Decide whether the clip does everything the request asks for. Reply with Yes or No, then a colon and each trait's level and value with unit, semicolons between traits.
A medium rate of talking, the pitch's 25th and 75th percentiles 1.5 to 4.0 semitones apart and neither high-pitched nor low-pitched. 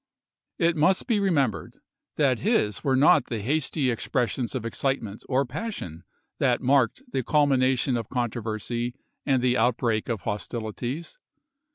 No: average, 145 wpm; average, 3.5 semitones; low, 130 Hz